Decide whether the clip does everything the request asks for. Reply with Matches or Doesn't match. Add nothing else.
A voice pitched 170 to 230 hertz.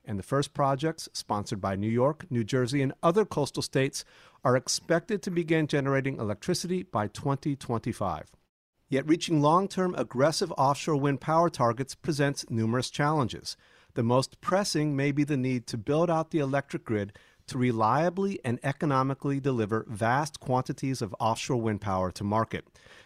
Doesn't match